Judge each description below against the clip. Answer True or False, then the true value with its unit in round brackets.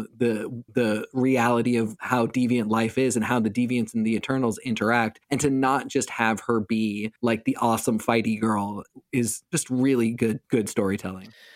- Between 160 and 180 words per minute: True (175 wpm)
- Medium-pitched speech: False (115 Hz)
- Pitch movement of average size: False (1.9 semitones)